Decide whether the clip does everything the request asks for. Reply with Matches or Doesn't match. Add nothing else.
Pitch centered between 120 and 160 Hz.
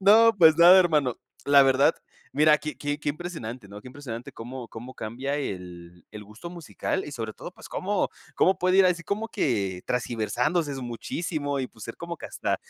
Matches